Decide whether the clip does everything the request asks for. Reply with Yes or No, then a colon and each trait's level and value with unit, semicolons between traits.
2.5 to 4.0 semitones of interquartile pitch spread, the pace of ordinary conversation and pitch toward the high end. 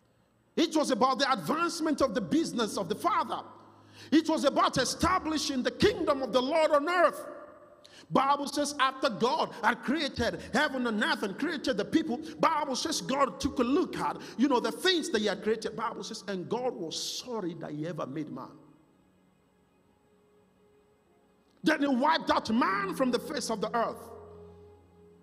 No: average, 4.9 semitones; average, 170 wpm; very high, 270 Hz